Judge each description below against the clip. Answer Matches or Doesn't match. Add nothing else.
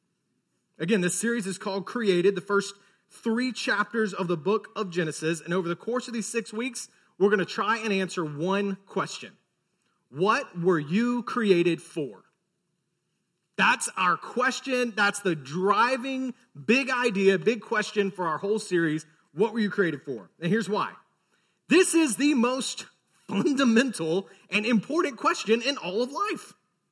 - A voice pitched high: Matches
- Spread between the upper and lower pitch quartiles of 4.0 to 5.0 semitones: Matches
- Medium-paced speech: Matches